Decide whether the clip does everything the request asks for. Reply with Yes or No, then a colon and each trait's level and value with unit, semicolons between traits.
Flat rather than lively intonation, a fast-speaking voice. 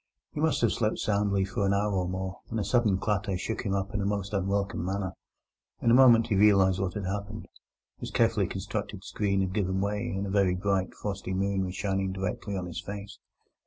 Yes: narrow, 1.4 semitones; fast, 215 wpm